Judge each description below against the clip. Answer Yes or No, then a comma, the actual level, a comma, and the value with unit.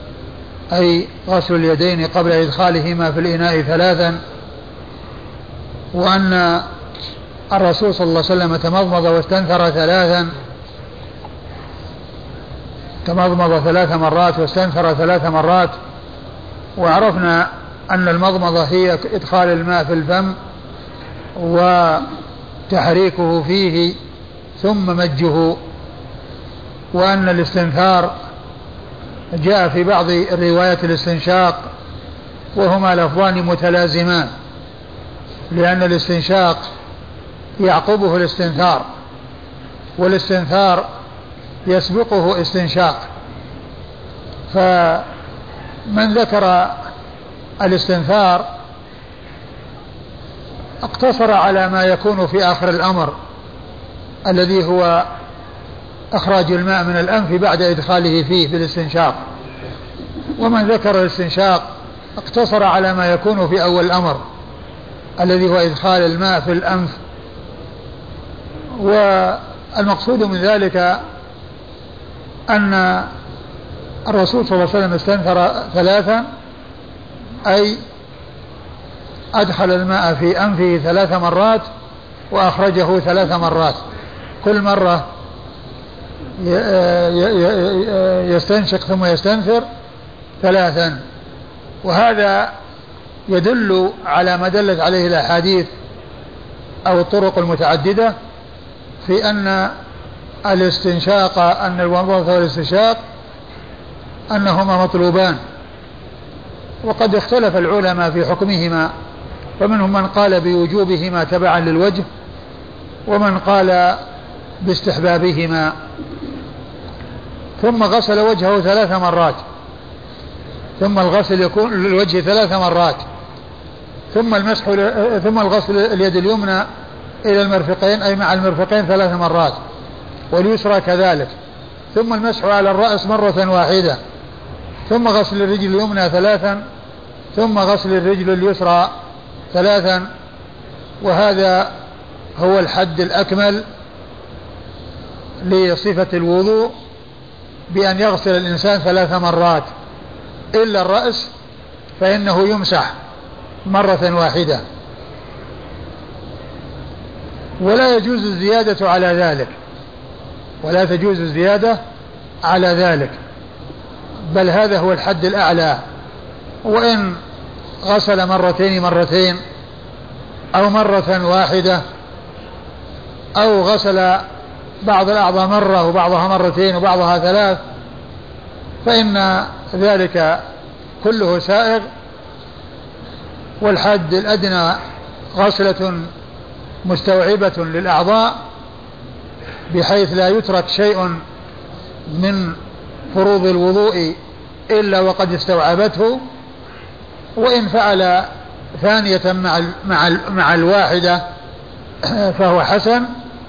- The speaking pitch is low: No, medium, 185 Hz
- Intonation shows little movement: Yes, narrow, 2.3 semitones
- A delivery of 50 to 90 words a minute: Yes, average, 80 wpm